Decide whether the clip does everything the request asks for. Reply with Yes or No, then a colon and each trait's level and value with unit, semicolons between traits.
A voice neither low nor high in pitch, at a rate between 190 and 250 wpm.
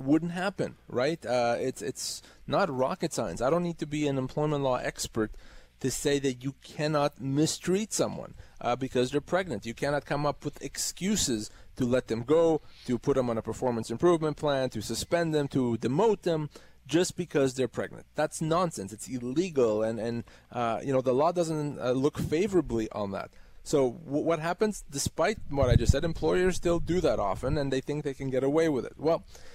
Yes: medium, 145 Hz; average, 200 wpm